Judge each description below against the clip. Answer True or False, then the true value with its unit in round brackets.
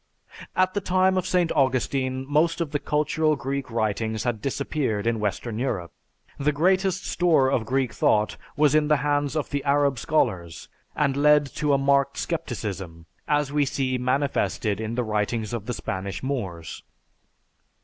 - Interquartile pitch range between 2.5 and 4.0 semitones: False (4.9 semitones)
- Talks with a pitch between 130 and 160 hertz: True (135 Hz)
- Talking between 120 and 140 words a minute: False (160 wpm)